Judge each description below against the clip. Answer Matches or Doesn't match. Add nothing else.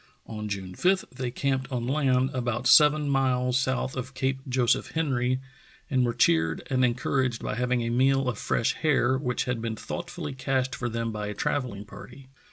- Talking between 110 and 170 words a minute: Doesn't match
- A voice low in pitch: Matches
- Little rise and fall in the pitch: Matches